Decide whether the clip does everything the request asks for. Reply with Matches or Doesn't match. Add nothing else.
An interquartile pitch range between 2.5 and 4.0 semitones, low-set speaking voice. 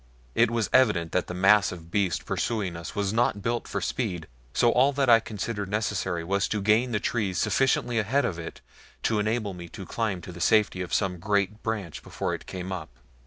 Matches